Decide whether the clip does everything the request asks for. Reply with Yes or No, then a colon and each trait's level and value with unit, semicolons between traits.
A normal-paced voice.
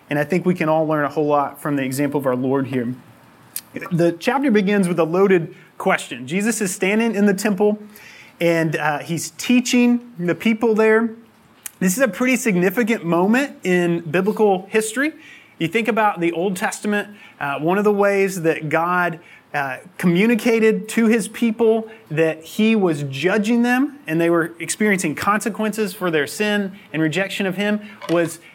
Yes: average, 170 wpm